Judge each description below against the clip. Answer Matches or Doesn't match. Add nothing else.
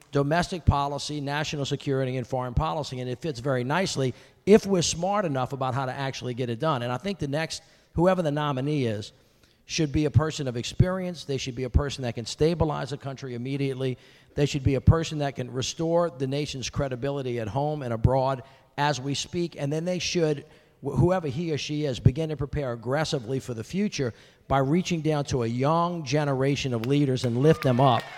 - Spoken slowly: Doesn't match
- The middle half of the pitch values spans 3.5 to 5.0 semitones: Doesn't match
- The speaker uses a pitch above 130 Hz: Matches